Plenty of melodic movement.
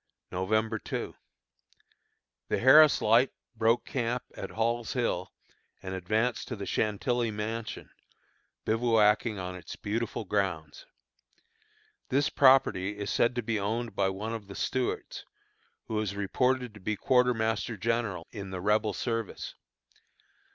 No: average, 2.9 semitones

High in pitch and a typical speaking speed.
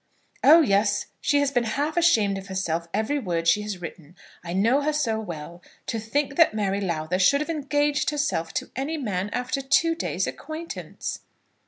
Yes: high, 220 Hz; average, 180 wpm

